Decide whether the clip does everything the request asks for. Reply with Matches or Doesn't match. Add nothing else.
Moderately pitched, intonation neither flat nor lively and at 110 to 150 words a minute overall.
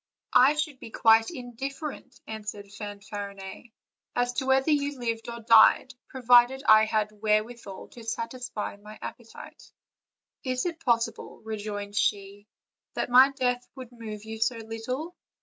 Doesn't match